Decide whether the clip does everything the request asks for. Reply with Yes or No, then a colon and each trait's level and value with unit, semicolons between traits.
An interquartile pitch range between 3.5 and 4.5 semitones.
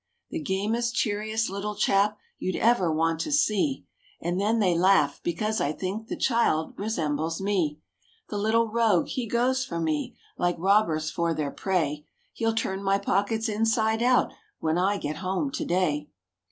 No: average, 4.9 semitones